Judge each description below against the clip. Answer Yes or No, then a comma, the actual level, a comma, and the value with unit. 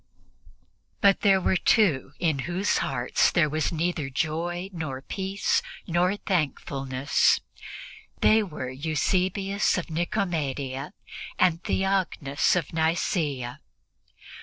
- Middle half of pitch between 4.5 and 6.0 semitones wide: Yes, average, 4.8 semitones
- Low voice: No, medium, 165 Hz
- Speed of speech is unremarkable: No, slow, 100 wpm